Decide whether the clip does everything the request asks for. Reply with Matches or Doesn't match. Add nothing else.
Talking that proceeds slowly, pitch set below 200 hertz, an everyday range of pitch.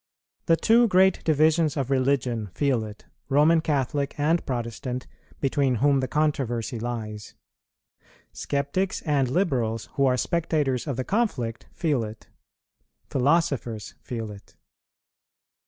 Matches